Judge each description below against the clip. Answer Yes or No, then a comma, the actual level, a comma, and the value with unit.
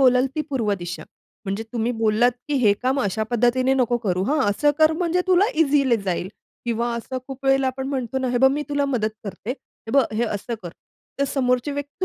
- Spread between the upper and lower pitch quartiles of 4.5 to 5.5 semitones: No, average, 3.5 semitones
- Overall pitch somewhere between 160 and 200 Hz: No, very high, 255 Hz